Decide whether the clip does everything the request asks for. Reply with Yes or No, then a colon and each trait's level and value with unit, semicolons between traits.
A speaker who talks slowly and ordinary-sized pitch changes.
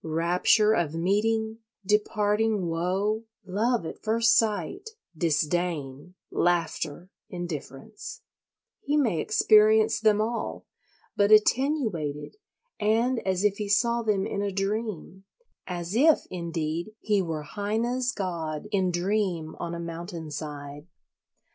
Yes: slow, 110 wpm; average, 4.5 semitones